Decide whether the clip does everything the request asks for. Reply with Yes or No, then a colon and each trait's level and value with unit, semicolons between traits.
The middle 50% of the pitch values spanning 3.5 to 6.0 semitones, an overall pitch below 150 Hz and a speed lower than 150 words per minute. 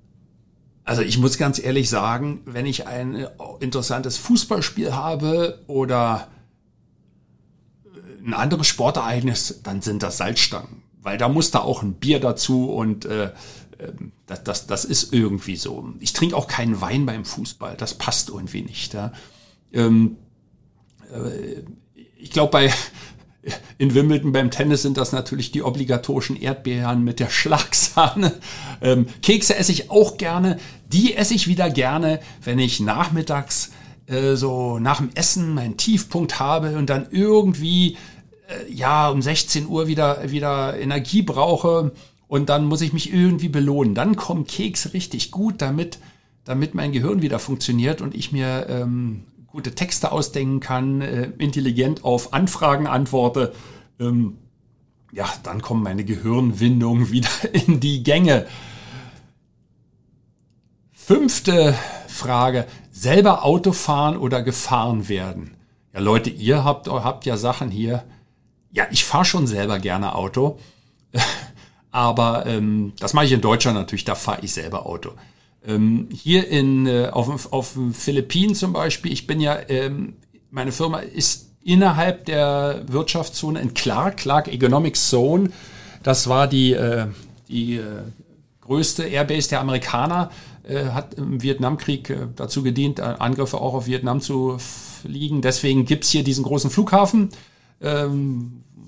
Yes: average, 3.9 semitones; low, 135 Hz; average, 135 wpm